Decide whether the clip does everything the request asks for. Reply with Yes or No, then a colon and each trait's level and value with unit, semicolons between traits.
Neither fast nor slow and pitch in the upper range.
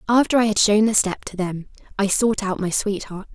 No: fast, 235 wpm; high, 205 Hz